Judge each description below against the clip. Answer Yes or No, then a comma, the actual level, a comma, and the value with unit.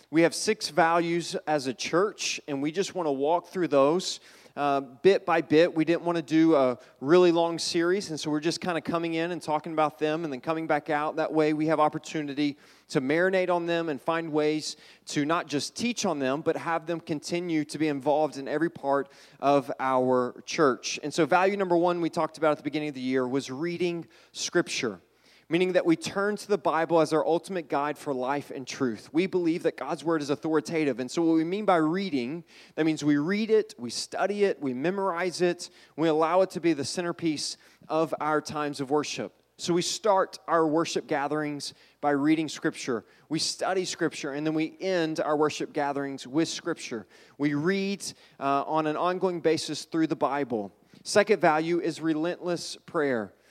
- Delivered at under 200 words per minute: No, fast, 205 wpm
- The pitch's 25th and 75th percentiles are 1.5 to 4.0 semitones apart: Yes, average, 2.8 semitones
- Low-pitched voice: No, medium, 160 Hz